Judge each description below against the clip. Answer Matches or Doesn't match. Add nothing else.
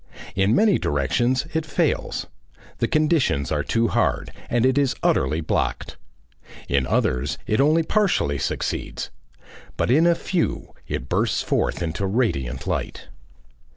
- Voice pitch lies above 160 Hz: Doesn't match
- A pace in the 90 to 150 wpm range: Matches